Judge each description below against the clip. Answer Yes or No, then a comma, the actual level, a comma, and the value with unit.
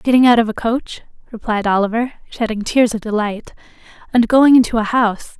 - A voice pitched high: Yes, high, 230 Hz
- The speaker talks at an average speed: Yes, average, 180 wpm